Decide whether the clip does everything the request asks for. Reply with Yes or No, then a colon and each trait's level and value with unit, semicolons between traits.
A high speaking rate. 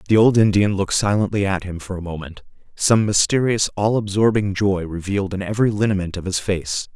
No: average, 190 wpm